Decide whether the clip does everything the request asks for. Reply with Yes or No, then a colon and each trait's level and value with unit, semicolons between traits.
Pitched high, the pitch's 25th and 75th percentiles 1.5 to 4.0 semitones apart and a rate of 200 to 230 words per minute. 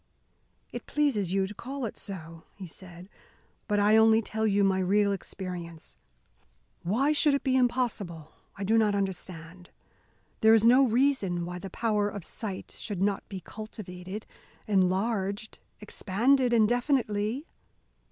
No: high, 205 Hz; average, 3.5 semitones; average, 140 wpm